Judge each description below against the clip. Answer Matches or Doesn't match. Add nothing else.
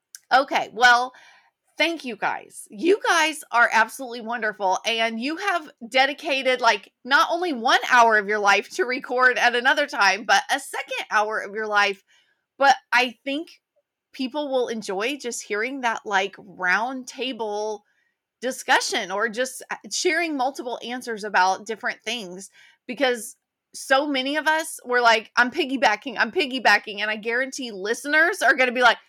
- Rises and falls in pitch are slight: Doesn't match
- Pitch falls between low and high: Doesn't match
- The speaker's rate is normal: Matches